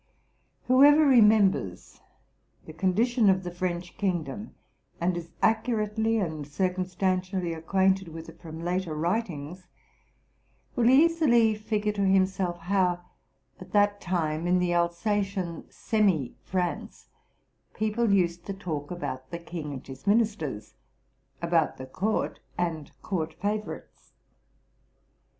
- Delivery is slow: Yes, slow, 120 wpm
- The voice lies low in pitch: No, medium, 185 Hz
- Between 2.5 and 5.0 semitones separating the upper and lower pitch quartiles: Yes, average, 3.8 semitones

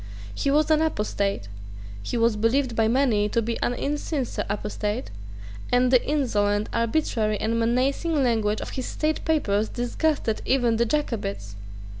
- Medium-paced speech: Yes, average, 145 wpm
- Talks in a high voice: Yes, high, 235 Hz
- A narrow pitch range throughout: No, average, 4.6 semitones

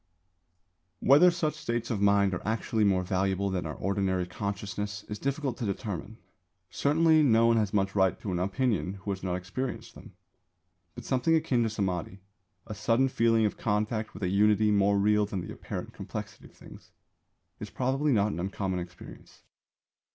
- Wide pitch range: No, average, 3.5 semitones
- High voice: No, low, 105 Hz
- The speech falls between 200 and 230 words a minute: No, average, 175 wpm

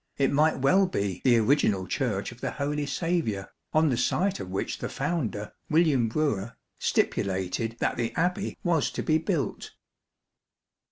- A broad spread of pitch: Yes, wide, 7.1 semitones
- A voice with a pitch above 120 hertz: Yes, low, 135 Hz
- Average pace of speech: Yes, average, 155 wpm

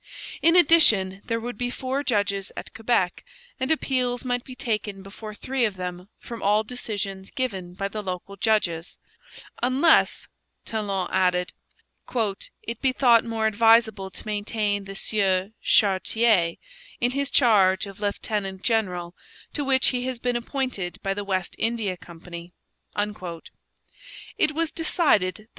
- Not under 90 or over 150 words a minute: Yes, average, 145 wpm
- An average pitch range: Yes, average, 4.3 semitones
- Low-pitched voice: No, high, 215 Hz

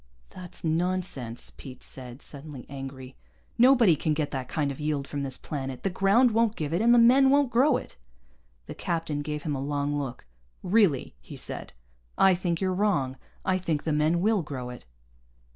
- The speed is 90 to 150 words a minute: No, average, 185 wpm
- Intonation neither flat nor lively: No, wide, 5.7 semitones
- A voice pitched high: No, medium, 155 Hz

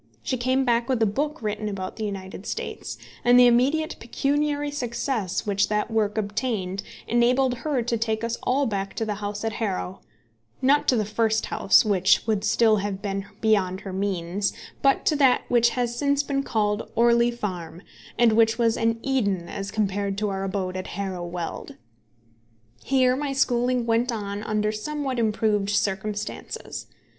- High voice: Yes, high, 220 Hz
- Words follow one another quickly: No, average, 170 wpm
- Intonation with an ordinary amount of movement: Yes, average, 3.6 semitones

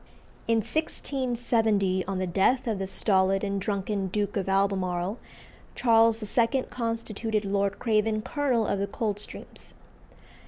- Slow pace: Yes, slow, 125 wpm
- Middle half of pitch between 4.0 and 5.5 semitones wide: No, average, 2.7 semitones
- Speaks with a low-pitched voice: No, high, 210 Hz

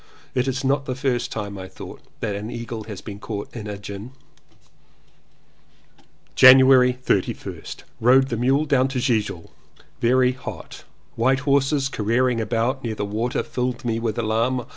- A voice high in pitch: No, low, 120 Hz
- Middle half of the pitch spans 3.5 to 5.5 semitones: No, average, 3.1 semitones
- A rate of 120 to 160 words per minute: Yes, average, 155 wpm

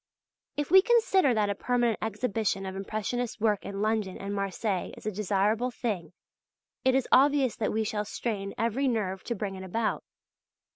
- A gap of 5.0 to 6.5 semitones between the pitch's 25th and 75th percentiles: No, average, 3.6 semitones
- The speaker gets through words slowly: No, average, 175 wpm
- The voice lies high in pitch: Yes, high, 215 Hz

